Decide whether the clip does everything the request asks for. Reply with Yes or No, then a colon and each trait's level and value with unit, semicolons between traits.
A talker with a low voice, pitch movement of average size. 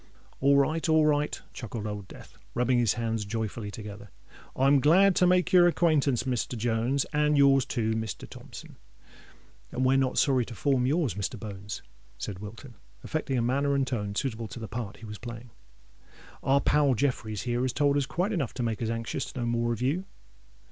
Yes: low, 125 Hz; average, 4.0 semitones